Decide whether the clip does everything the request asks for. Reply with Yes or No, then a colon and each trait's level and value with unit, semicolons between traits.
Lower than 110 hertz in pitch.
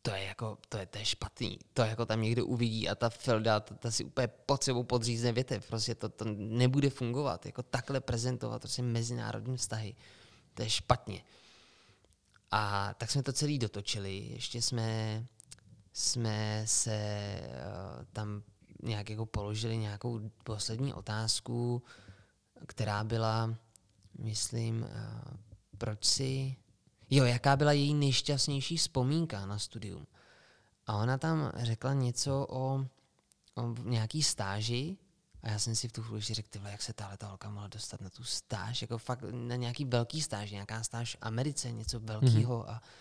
No: low, 115 Hz